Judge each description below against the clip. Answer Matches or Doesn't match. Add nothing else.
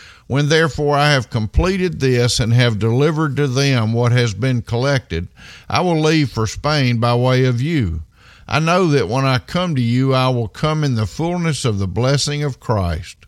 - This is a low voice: Matches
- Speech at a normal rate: Matches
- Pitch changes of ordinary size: Matches